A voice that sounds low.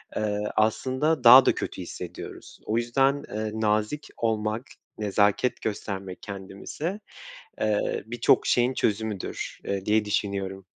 Yes: low, 110 Hz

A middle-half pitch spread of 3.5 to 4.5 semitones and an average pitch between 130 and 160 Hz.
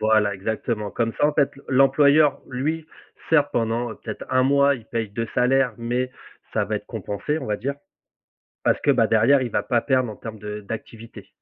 No: average, 3.8 semitones; low, 120 Hz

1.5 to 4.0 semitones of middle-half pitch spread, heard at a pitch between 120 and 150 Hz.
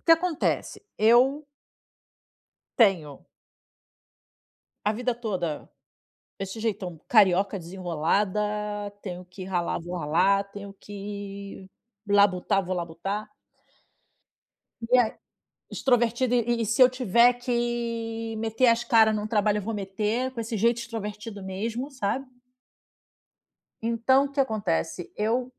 No: average, 3.6 semitones; high, 215 Hz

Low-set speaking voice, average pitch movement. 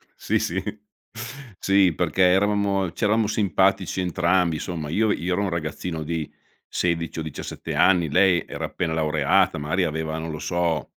Yes: very low, 85 Hz; average, 3.1 semitones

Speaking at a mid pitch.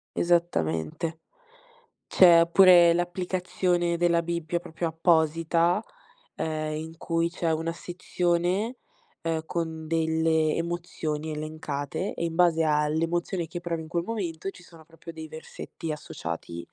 Yes: medium, 165 Hz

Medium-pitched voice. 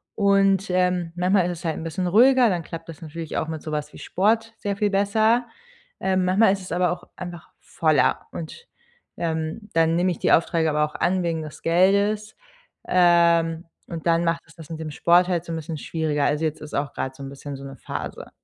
Yes: medium, 170 Hz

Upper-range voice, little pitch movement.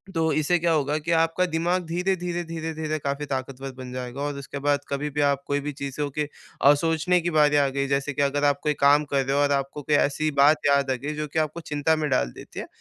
No: medium, 145 Hz; narrow, 2.2 semitones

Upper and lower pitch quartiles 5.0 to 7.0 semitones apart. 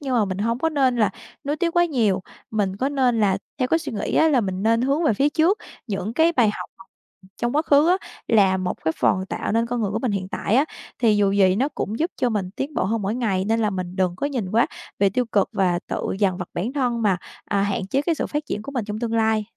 Yes: wide, 5.4 semitones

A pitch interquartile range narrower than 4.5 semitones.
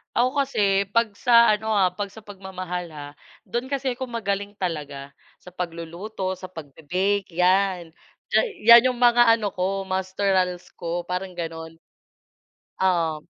Yes: average, 3.4 semitones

